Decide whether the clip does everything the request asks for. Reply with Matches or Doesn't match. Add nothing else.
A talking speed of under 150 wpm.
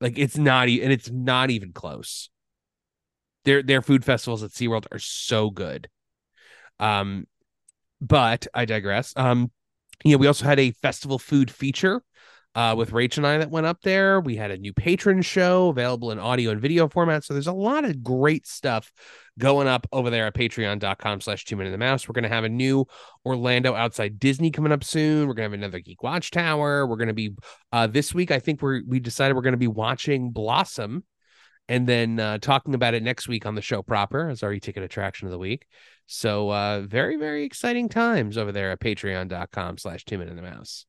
Doesn't match